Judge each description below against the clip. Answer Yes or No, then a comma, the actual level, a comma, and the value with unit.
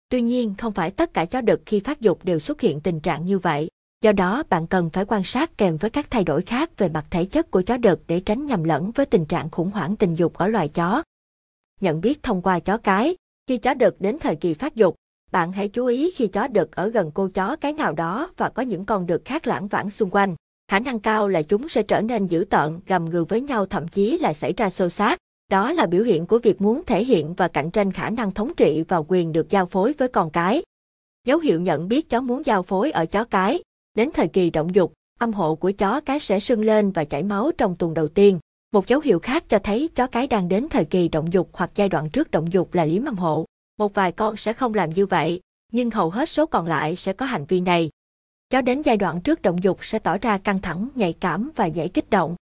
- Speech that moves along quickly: Yes, fast, 260 wpm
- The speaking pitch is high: Yes, high, 200 Hz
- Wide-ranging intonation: No, average, 5.0 semitones